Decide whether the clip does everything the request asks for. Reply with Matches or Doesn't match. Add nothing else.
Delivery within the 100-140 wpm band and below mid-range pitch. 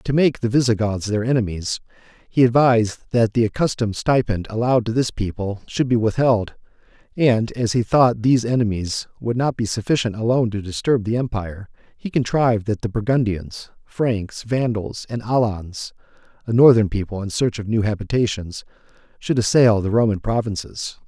Doesn't match